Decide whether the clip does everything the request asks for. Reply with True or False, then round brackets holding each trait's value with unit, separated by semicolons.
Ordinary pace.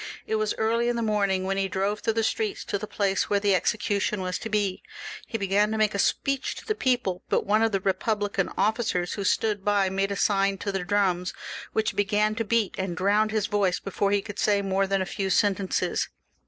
False (225 wpm)